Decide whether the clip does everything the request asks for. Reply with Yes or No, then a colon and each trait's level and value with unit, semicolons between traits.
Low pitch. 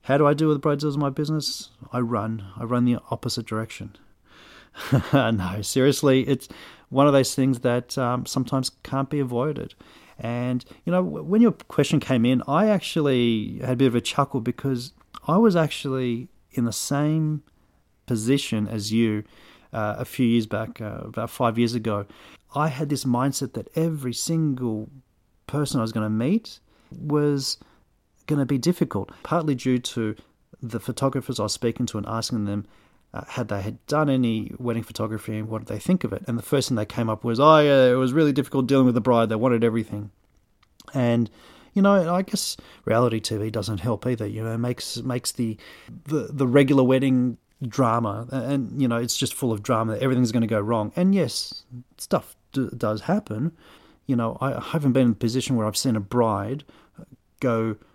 Yes: low, 125 Hz